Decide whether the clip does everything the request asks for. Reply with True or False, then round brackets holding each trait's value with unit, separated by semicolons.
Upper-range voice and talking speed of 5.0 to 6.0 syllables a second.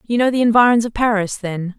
True (220 Hz; 5.9 syllables/s)